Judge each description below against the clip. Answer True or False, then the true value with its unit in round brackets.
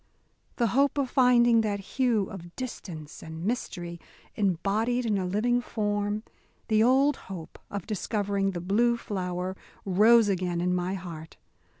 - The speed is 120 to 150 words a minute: True (140 wpm)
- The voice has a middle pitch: False (205 Hz)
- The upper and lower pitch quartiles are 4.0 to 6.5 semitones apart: True (4.6 semitones)